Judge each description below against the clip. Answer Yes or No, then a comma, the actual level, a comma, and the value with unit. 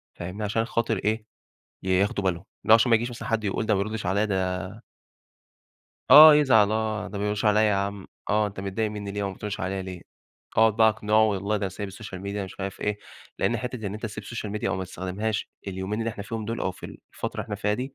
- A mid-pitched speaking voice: No, low, 105 Hz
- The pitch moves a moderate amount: No, narrow, 2.0 semitones